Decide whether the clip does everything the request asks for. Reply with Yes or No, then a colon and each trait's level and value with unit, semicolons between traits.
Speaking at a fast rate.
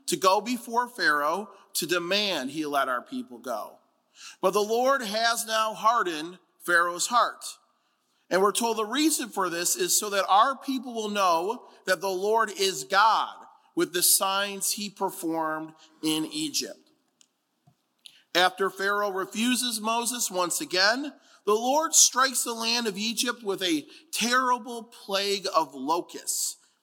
No: average, 145 wpm